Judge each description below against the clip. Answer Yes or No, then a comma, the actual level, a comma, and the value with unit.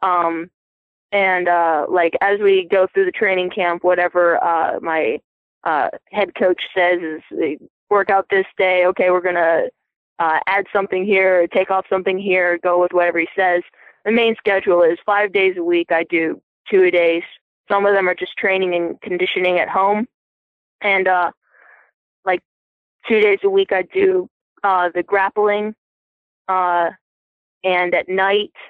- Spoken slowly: No, average, 165 wpm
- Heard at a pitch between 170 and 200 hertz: Yes, medium, 185 Hz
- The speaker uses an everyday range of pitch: No, narrow, 2.0 semitones